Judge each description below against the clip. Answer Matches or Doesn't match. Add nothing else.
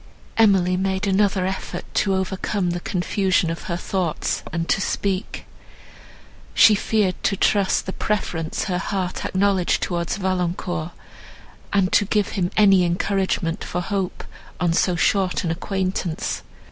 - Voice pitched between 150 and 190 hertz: Matches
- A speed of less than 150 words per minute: Matches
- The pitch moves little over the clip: Matches